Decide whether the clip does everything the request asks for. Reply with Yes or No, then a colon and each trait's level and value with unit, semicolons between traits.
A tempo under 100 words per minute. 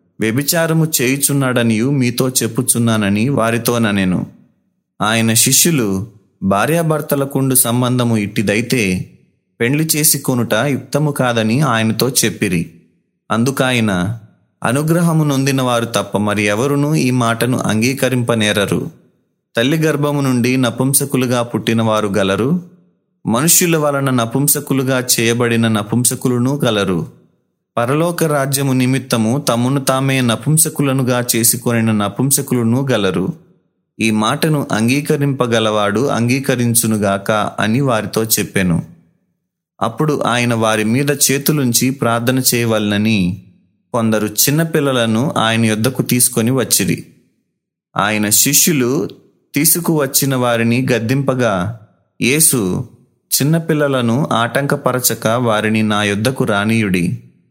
Yes: average, 85 wpm